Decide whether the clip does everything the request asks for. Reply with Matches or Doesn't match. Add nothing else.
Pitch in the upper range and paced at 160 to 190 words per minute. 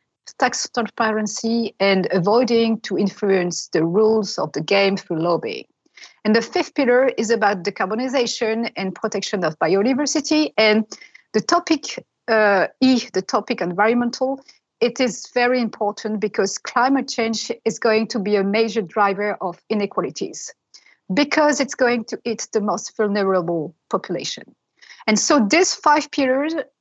Doesn't match